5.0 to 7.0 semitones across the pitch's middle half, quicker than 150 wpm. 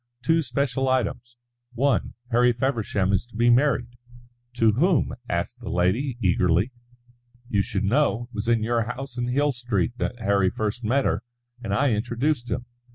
No: average, 3.3 semitones; average, 165 wpm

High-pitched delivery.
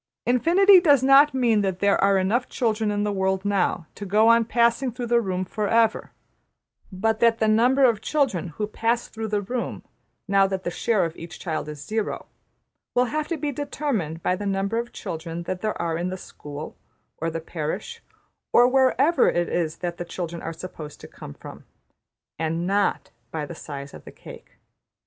Yes: high, 205 Hz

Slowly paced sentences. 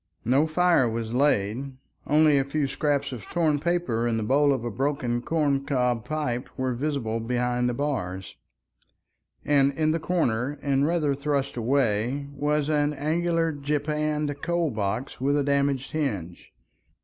No: average, 150 wpm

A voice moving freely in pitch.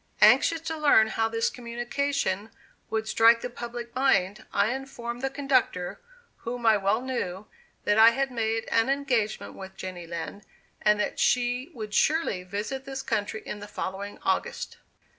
No: average, 3.9 semitones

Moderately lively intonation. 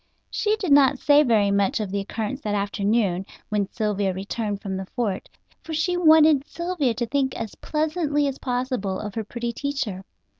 No: wide, 6.2 semitones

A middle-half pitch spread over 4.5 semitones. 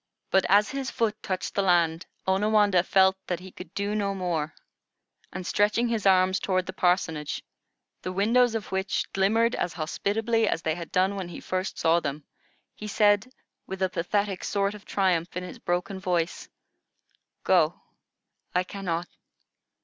No: narrow, 2.5 semitones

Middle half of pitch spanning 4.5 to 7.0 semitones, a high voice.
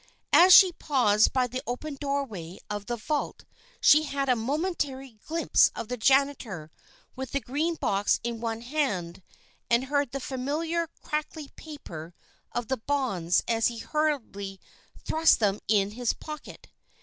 Yes: average, 5.1 semitones; very high, 260 Hz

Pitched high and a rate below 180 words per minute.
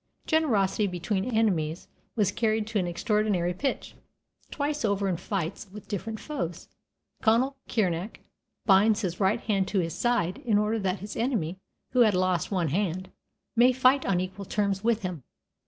Yes: high, 205 Hz; average, 160 wpm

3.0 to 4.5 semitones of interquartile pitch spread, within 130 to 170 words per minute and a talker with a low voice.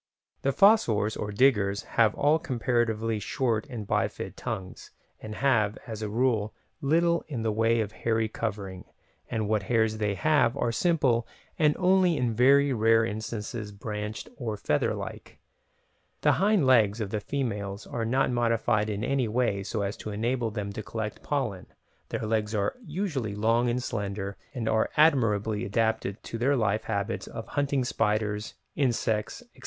Yes: average, 3.4 semitones; average, 165 wpm; low, 115 Hz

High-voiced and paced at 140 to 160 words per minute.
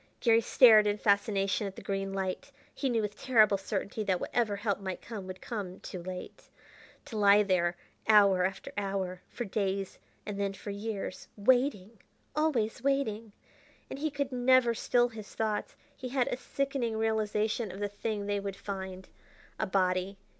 No: high, 205 Hz; average, 170 wpm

